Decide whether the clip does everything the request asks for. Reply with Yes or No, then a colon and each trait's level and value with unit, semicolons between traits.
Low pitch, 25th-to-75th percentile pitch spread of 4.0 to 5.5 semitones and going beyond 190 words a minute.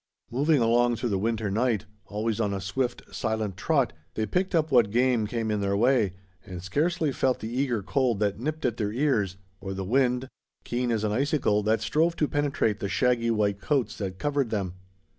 Yes: low, 115 Hz; average, 4.3 semitones; average, 200 wpm